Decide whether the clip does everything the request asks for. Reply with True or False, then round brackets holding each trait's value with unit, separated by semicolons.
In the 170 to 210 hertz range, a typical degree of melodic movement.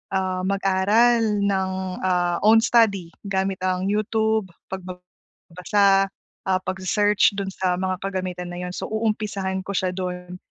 False (190 Hz; 2.1 semitones)